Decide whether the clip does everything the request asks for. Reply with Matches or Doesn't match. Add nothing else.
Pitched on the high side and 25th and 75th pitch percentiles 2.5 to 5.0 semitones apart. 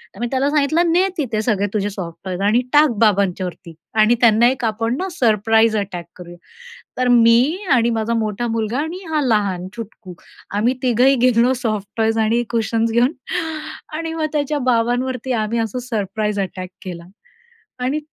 Matches